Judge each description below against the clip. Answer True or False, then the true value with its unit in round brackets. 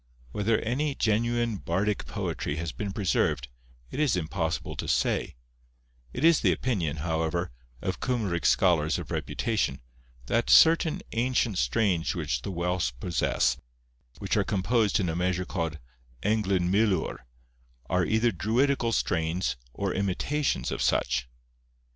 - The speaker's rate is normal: False (130 wpm)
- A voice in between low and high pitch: False (95 Hz)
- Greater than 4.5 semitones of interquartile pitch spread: True (5.4 semitones)